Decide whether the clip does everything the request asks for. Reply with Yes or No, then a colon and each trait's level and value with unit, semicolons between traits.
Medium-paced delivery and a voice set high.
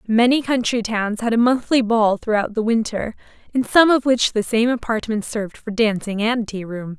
Yes: average, 195 wpm; high, 225 Hz